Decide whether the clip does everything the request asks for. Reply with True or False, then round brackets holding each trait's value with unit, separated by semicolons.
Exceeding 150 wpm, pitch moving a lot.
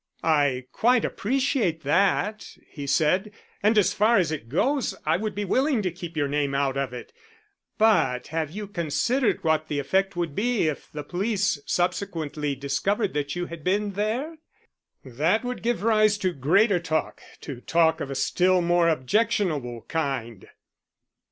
True (160 wpm; 6.1 semitones)